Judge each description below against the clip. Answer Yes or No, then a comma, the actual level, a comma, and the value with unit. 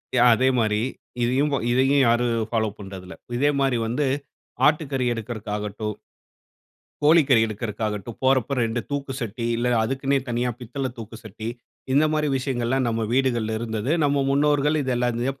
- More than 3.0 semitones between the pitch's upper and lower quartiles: Yes, average, 3.4 semitones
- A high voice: No, low, 120 Hz